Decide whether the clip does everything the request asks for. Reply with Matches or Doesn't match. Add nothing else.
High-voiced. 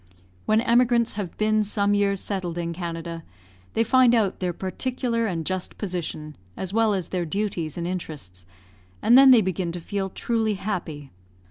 Matches